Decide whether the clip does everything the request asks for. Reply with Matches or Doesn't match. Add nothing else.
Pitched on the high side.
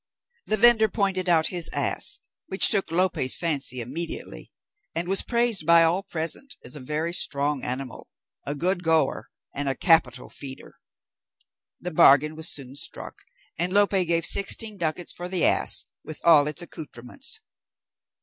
Doesn't match